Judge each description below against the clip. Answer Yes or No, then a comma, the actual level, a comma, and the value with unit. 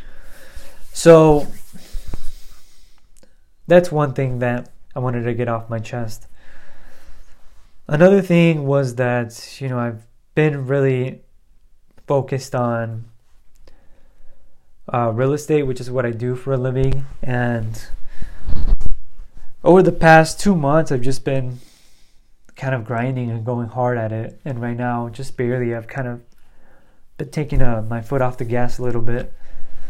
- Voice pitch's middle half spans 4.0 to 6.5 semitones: No, average, 2.9 semitones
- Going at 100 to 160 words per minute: Yes, average, 140 wpm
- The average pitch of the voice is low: Yes, low, 125 Hz